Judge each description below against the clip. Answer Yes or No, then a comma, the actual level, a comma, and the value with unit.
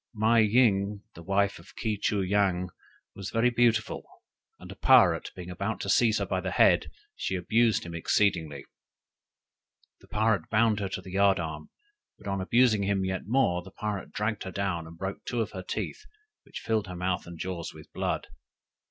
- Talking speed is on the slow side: No, average, 185 wpm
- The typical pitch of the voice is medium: No, low, 100 Hz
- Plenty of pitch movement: No, average, 3.1 semitones